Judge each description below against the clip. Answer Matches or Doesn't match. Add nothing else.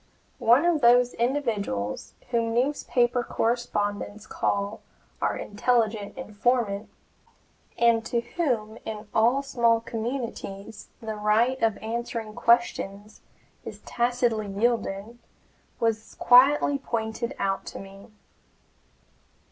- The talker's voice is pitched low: Doesn't match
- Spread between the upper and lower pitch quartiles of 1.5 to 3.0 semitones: Matches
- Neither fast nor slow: Doesn't match